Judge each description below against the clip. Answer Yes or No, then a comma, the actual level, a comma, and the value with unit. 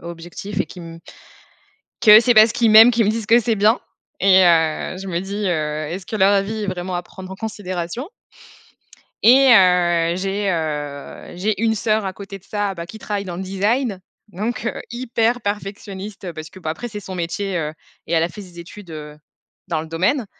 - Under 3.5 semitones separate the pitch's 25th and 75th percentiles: No, average, 3.8 semitones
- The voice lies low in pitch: No, high, 195 Hz